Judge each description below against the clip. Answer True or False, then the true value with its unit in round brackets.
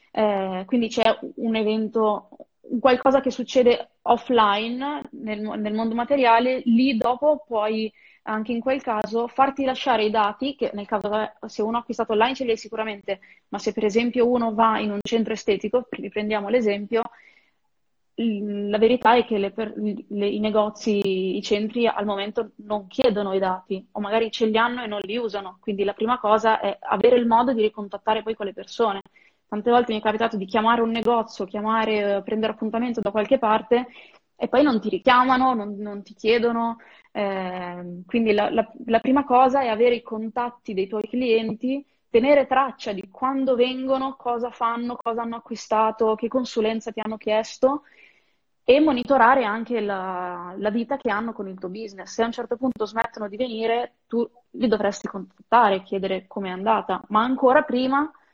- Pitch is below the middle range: False (225 Hz)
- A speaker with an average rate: False (175 wpm)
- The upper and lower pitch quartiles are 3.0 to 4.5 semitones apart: False (2.4 semitones)